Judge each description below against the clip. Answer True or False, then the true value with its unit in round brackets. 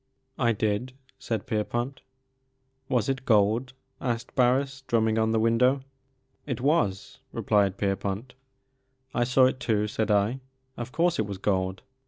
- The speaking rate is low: True (125 wpm)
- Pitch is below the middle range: True (115 Hz)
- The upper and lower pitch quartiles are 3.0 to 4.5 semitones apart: True (3.6 semitones)